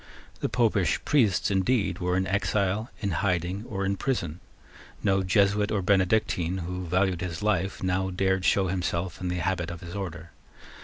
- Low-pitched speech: Yes, very low, 95 Hz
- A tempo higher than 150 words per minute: Yes, average, 170 wpm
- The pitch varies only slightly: Yes, narrow, 2.0 semitones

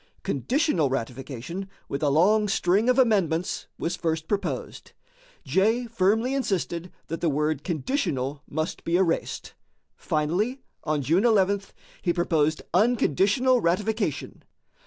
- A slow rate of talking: Yes, slow, 115 wpm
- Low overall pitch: No, medium, 180 Hz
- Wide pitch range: Yes, wide, 5.8 semitones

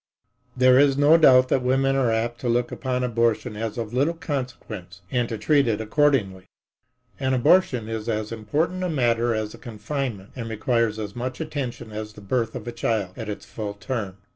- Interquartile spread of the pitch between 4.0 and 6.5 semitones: No, average, 3.4 semitones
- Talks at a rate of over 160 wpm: Yes, average, 190 wpm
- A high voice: No, low, 120 Hz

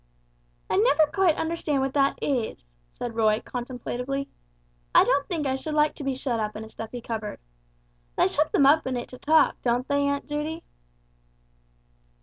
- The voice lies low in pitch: No, very high, 275 Hz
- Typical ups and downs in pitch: Yes, average, 3.8 semitones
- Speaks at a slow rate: No, average, 175 wpm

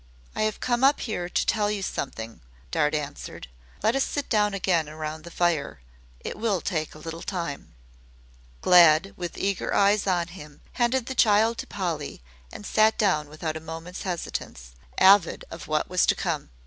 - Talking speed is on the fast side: No, average, 175 wpm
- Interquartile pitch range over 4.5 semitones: Yes, average, 5.0 semitones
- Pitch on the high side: No, medium, 180 Hz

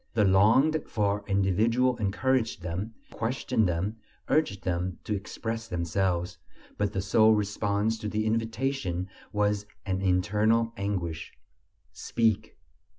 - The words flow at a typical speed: No, slow, 115 wpm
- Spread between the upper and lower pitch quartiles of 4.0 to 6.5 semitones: No, average, 2.9 semitones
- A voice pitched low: Yes, low, 105 Hz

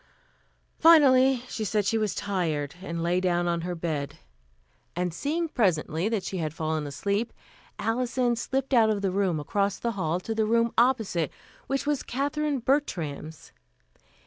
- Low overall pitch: No, high, 200 Hz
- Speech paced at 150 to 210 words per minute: Yes, average, 155 wpm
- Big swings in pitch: Yes, wide, 6.5 semitones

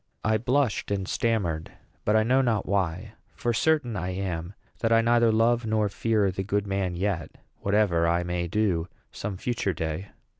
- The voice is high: No, low, 100 Hz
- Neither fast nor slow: Yes, average, 175 wpm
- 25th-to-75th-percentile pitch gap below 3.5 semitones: No, average, 3.9 semitones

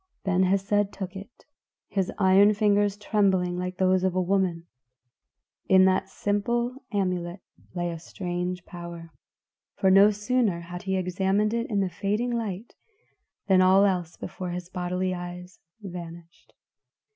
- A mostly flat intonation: Yes, narrow, 2.2 semitones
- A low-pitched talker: No, high, 190 Hz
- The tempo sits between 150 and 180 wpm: No, average, 140 wpm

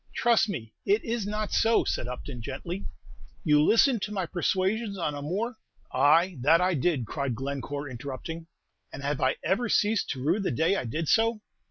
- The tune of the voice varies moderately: No, wide, 7.0 semitones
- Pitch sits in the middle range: Yes, medium, 165 Hz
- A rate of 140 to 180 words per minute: No, average, 190 wpm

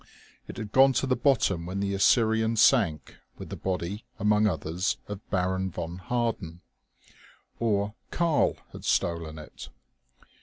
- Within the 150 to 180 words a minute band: No, average, 140 wpm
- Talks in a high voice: No, low, 100 Hz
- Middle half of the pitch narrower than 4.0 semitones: No, average, 4.4 semitones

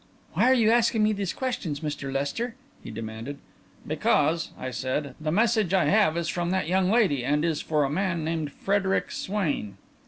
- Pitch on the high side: No, medium, 170 Hz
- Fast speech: No, average, 185 wpm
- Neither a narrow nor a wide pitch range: No, wide, 5.9 semitones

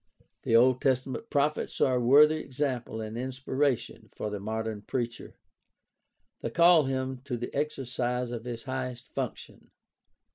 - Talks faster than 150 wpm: No, average, 140 wpm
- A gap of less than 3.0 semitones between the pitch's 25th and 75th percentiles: Yes, narrow, 2.6 semitones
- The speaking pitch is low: Yes, low, 130 Hz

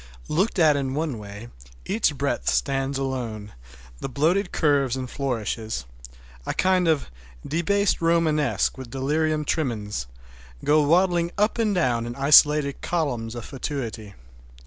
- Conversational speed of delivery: No, slow, 125 wpm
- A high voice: No, medium, 140 Hz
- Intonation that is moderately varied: No, wide, 6.0 semitones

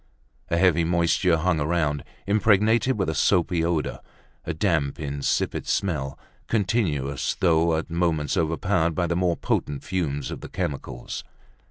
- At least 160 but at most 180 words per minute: No, average, 140 wpm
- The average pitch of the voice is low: Yes, very low, 85 Hz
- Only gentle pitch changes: No, average, 3.5 semitones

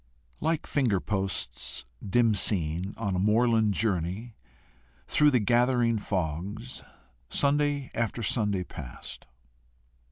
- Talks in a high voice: No, low, 110 Hz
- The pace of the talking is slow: Yes, slow, 100 wpm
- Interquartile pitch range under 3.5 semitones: No, average, 4.3 semitones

